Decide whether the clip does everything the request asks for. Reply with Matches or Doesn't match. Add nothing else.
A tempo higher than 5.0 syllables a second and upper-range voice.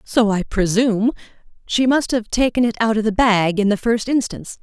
Matches